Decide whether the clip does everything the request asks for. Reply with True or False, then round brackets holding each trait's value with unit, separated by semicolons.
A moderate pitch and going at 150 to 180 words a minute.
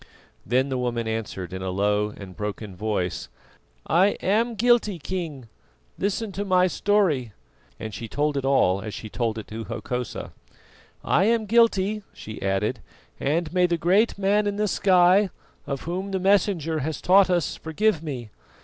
True (160 Hz; 165 wpm)